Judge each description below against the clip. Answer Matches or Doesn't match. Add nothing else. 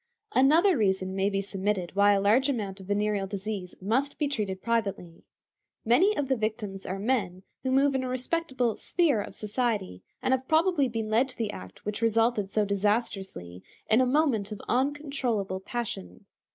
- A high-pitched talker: Matches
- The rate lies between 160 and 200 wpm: Matches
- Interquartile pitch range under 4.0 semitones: Doesn't match